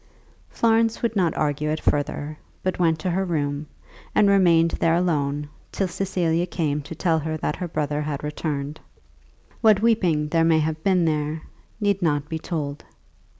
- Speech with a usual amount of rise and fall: Yes, average, 3.4 semitones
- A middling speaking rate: Yes, average, 165 wpm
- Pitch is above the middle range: No, medium, 160 Hz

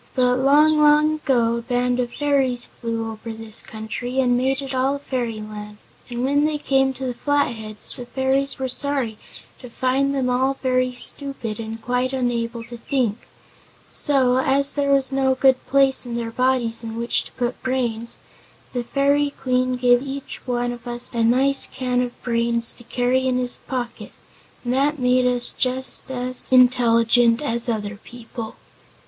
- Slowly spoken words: No, average, 170 wpm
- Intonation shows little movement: Yes, narrow, 2.2 semitones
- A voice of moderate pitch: No, very high, 250 Hz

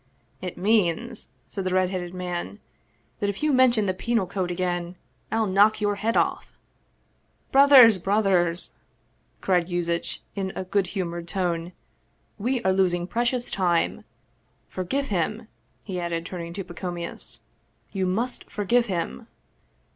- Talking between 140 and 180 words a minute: Yes, average, 160 wpm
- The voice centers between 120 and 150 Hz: No, medium, 185 Hz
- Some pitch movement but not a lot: Yes, average, 3.6 semitones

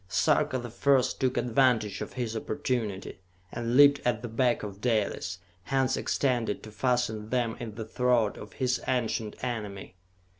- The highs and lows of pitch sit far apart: No, average, 2.8 semitones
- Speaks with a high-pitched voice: No, low, 120 Hz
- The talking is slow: No, average, 155 wpm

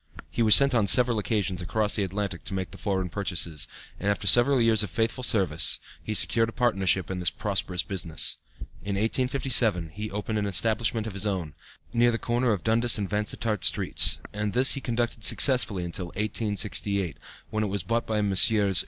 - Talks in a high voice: No, low, 105 Hz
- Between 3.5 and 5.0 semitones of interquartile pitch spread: No, average, 3.1 semitones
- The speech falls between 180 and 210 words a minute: Yes, average, 190 wpm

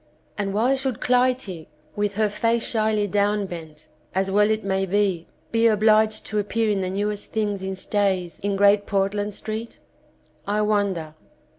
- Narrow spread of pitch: Yes, narrow, 1.9 semitones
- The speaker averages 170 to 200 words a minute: No, average, 155 wpm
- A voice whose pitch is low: No, high, 205 Hz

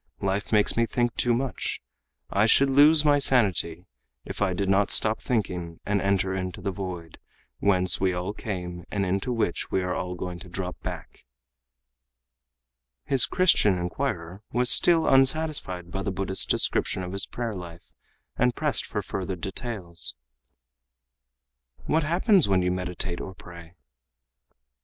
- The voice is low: Yes, very low, 95 Hz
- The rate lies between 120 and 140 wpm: No, average, 150 wpm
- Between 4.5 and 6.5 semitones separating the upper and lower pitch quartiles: Yes, average, 5.0 semitones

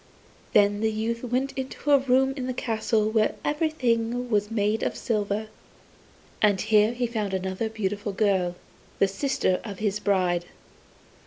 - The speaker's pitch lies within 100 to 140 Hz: No, high, 220 Hz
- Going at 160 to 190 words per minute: No, average, 150 wpm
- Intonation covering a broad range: No, average, 3.3 semitones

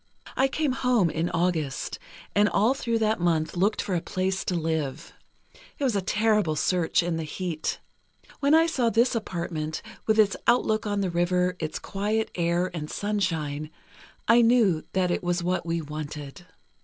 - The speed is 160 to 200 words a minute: Yes, average, 170 wpm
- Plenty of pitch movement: No, average, 4.9 semitones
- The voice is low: No, medium, 180 Hz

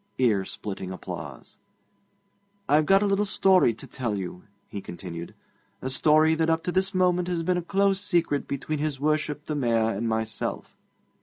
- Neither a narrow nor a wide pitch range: No, wide, 8.0 semitones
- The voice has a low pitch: No, medium, 150 Hz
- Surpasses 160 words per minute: Yes, average, 170 wpm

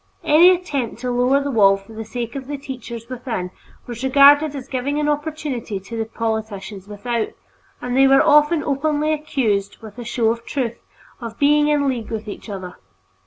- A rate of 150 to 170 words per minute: No, average, 185 wpm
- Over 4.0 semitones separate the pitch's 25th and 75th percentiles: Yes, average, 4.4 semitones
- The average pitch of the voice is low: No, very high, 250 Hz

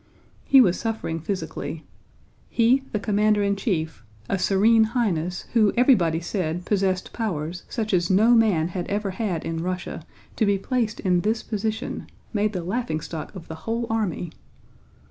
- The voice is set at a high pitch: Yes, high, 200 Hz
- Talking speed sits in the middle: Yes, average, 150 wpm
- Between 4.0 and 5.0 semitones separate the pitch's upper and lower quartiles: Yes, average, 4.3 semitones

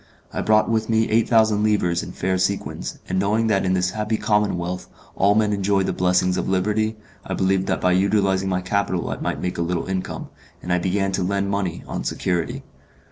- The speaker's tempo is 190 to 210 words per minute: Yes, fast, 205 wpm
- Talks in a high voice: No, very low, 95 Hz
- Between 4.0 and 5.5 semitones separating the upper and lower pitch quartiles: No, narrow, 2.4 semitones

